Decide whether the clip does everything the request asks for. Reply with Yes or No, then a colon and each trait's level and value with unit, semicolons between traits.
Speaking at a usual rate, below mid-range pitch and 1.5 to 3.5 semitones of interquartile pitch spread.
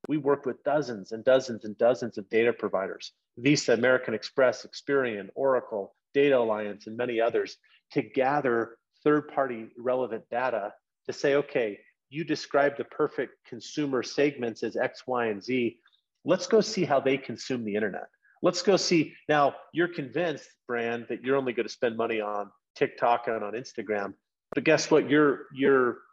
No: average, 165 wpm; low, 130 Hz; average, 3.9 semitones